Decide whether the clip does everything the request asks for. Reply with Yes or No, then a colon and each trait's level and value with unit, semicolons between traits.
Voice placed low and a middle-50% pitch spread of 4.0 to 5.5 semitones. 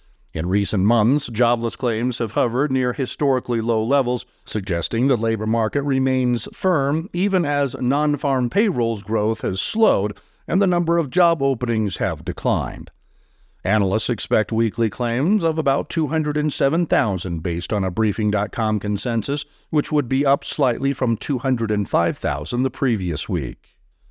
Yes: low, 125 Hz; average, 4.6 semitones